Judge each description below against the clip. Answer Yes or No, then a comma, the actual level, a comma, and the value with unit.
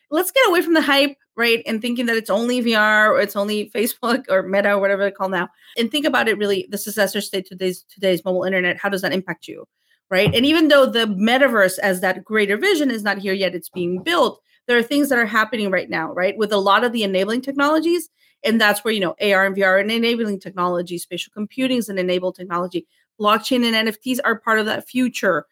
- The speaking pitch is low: No, high, 210 Hz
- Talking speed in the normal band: No, fast, 235 wpm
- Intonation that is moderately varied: Yes, average, 4.1 semitones